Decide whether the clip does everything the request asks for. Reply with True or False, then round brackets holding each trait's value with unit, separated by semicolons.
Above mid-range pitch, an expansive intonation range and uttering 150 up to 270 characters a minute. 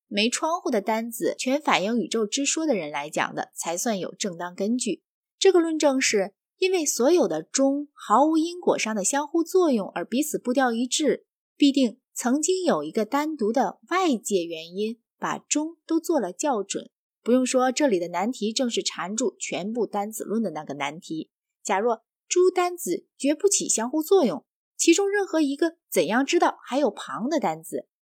True (265 Hz; 6.9 semitones; 265 characters per minute)